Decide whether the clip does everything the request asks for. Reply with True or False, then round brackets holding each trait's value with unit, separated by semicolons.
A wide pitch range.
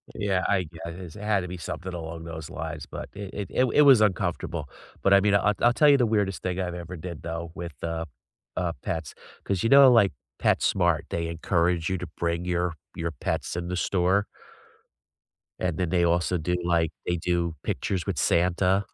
False (2.6 semitones)